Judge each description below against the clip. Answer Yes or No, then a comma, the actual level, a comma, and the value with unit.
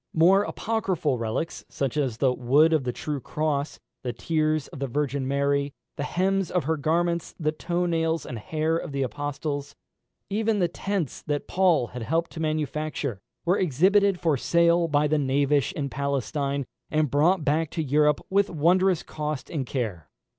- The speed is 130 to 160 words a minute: No, average, 170 wpm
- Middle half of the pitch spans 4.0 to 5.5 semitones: No, average, 3.4 semitones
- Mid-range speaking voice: Yes, medium, 150 Hz